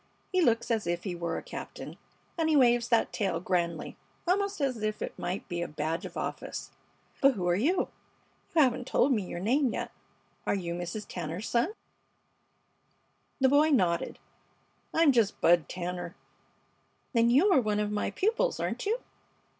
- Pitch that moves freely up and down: Yes, wide, 7.8 semitones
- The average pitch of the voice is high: Yes, high, 220 Hz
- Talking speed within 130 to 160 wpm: No, average, 170 wpm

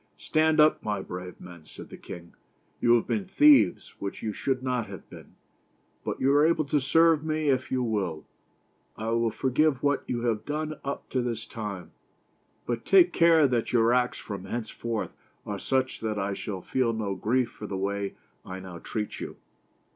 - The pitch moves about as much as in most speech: No, wide, 5.7 semitones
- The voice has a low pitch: Yes, low, 120 Hz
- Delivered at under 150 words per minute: No, average, 190 wpm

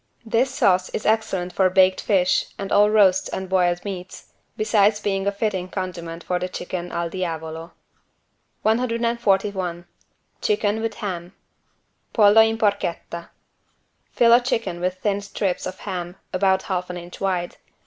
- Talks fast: No, average, 145 wpm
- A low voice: No, high, 190 Hz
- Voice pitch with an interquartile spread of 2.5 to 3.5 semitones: Yes, average, 2.8 semitones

